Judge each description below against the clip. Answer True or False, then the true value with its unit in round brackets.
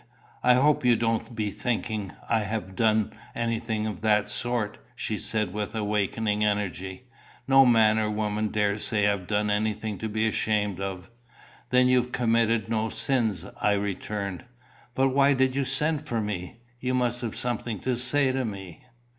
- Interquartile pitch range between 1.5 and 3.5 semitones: True (2.8 semitones)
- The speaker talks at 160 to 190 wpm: True (165 wpm)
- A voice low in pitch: True (110 Hz)